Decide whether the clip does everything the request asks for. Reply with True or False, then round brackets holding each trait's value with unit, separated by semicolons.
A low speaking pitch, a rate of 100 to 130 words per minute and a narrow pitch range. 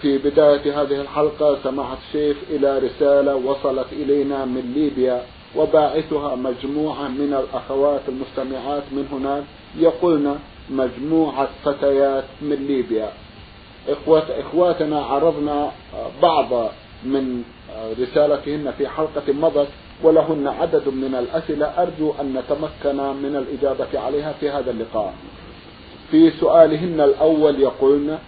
False (145 Hz; 105 wpm; 1.7 semitones)